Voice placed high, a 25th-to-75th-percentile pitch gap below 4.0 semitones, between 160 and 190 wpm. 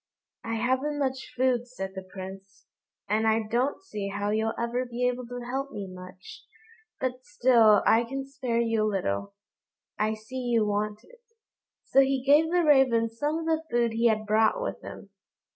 Yes: high, 235 Hz; average, 3.6 semitones; average, 180 wpm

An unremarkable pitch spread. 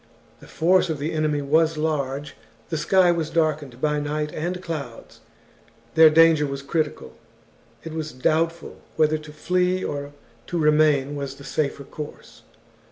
No: narrow, 2.1 semitones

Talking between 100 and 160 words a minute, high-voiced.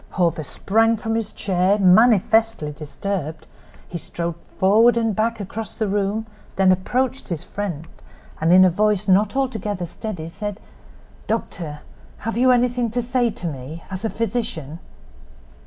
Yes: average, 140 wpm; high, 205 Hz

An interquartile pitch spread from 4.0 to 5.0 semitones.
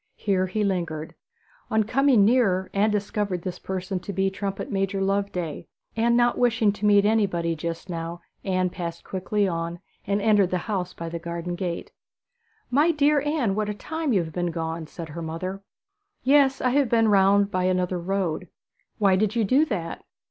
No: average, 3.5 semitones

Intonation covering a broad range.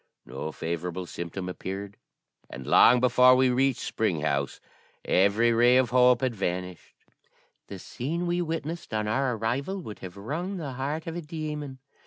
Yes: wide, 7.0 semitones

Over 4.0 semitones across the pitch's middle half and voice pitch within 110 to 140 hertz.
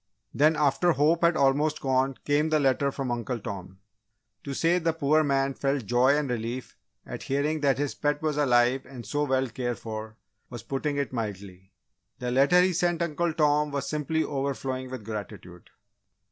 No: average, 3.4 semitones; low, 135 Hz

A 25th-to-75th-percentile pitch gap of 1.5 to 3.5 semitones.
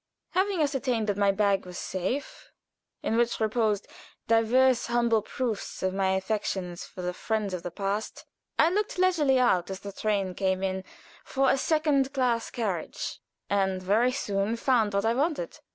No: average, 5.0 semitones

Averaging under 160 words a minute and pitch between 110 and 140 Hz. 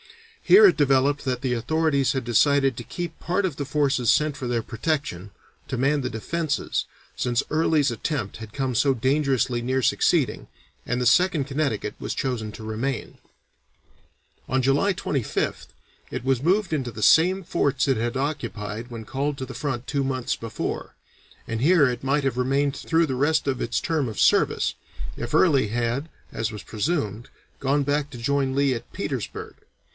No: average, 175 wpm; low, 135 Hz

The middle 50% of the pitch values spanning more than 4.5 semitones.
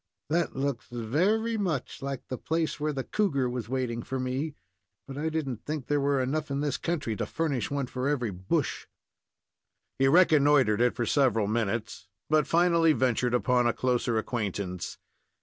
No: average, 4.2 semitones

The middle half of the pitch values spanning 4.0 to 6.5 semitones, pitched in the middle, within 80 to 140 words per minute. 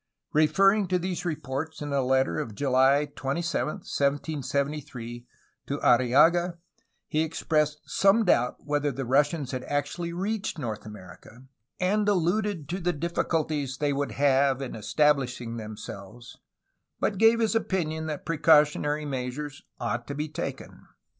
Yes: average, 4.3 semitones; medium, 145 Hz; slow, 135 wpm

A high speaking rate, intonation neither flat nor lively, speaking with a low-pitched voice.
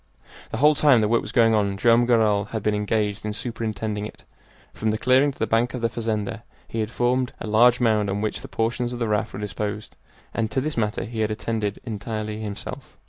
No: fast, 225 wpm; narrow, 2.0 semitones; low, 110 Hz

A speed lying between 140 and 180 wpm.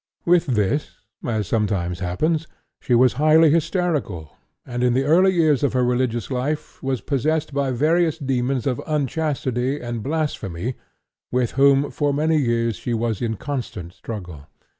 Yes: average, 150 wpm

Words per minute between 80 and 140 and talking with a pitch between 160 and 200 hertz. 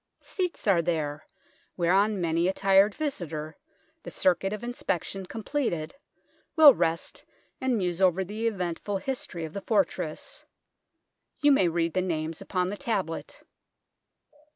Yes: slow, 135 wpm; medium, 185 Hz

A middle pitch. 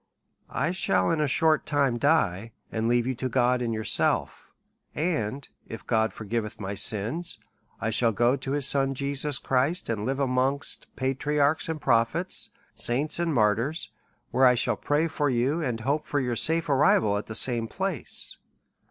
No: low, 130 Hz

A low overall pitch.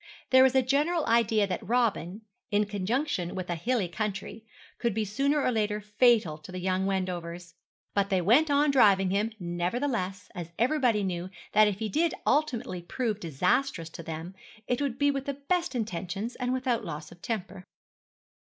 No: high, 210 Hz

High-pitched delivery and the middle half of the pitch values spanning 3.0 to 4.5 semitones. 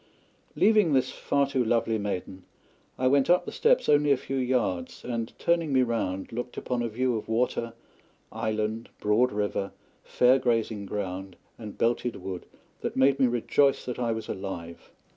No: low, 120 Hz; average, 3.8 semitones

